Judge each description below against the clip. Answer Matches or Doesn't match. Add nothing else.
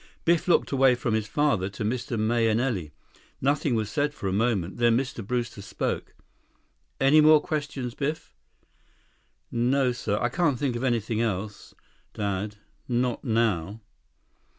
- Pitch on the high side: Doesn't match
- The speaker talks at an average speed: Doesn't match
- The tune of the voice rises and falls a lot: Doesn't match